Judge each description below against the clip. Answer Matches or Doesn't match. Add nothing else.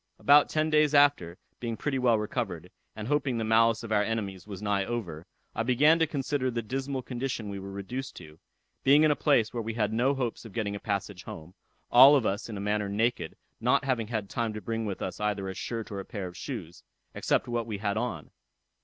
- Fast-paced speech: Matches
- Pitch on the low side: Matches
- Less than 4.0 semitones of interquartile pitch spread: Doesn't match